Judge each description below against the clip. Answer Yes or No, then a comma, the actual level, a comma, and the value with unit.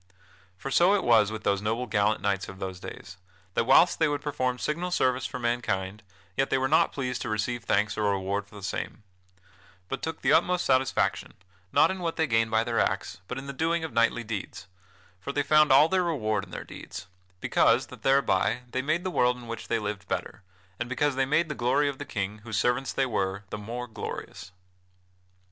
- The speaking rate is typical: No, fast, 215 wpm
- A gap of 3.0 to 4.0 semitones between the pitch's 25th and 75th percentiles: No, average, 4.9 semitones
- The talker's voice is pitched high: No, low, 125 Hz